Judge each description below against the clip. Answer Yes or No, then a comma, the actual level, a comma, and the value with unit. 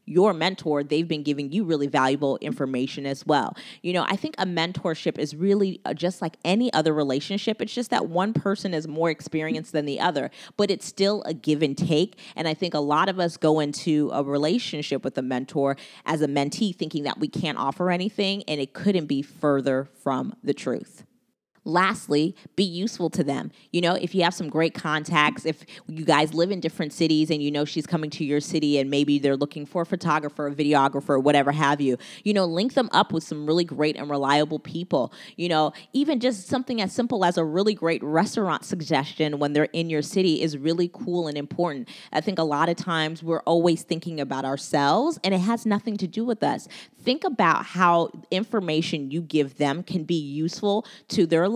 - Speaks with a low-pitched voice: No, medium, 165 Hz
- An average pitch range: Yes, average, 3.9 semitones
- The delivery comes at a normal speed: No, fast, 210 wpm